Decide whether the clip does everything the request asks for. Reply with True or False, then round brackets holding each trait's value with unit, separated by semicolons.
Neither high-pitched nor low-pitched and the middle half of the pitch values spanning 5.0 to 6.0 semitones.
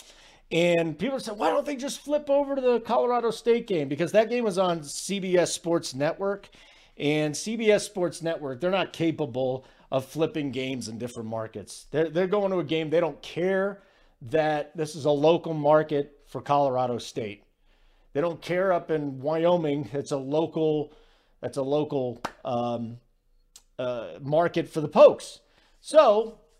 True (160 Hz; 5.3 semitones)